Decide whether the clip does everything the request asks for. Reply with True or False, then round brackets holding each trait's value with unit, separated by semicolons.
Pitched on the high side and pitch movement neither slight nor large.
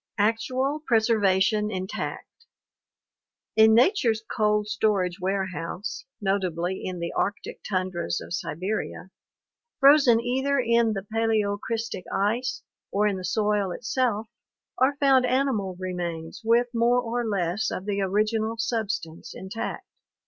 True (215 Hz; 3.6 semitones)